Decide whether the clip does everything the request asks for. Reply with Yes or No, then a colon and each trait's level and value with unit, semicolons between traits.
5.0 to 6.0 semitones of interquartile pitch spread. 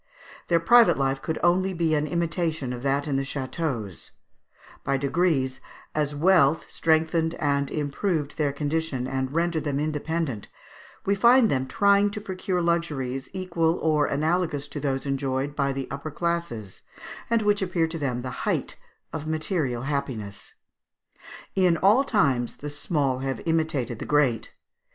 No: average, 4.0 semitones